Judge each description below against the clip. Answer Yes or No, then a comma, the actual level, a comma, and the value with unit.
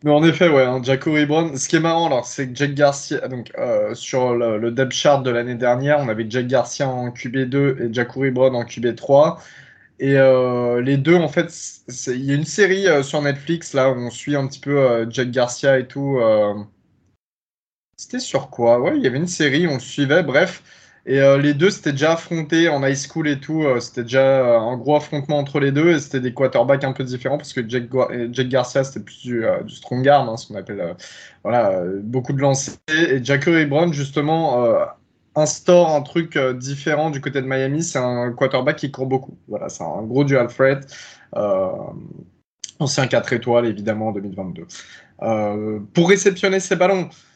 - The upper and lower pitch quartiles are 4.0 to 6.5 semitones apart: No, average, 3.5 semitones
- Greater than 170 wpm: Yes, average, 210 wpm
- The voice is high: No, low, 135 Hz